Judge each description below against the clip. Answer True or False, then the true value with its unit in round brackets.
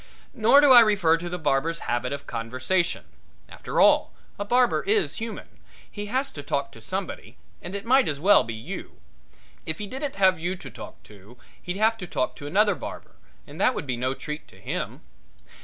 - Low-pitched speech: False (180 Hz)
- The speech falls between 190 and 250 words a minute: True (200 wpm)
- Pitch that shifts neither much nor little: False (7.7 semitones)